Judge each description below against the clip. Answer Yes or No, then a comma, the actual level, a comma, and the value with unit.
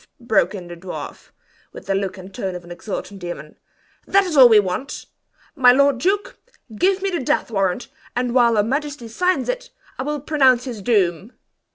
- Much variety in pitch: Yes, wide, 6.8 semitones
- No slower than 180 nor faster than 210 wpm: Yes, average, 190 wpm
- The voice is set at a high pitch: Yes, high, 235 Hz